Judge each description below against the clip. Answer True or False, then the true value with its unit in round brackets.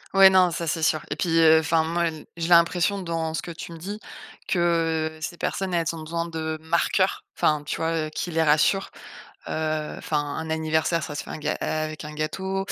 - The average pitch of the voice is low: False (160 Hz)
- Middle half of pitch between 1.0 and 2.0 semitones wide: True (1.5 semitones)